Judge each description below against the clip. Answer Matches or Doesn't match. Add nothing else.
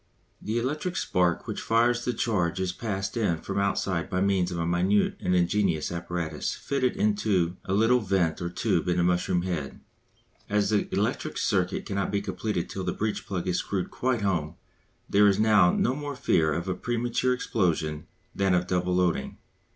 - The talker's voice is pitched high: Doesn't match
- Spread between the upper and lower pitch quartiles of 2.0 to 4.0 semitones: Matches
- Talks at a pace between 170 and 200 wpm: Matches